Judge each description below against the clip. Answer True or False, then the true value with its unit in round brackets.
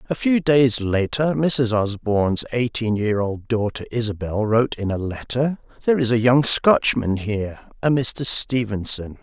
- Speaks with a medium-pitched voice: False (120 Hz)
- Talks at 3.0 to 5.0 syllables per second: True (4.5 syllables/s)